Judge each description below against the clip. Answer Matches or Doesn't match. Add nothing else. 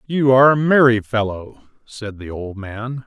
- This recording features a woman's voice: Doesn't match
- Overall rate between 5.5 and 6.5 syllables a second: Doesn't match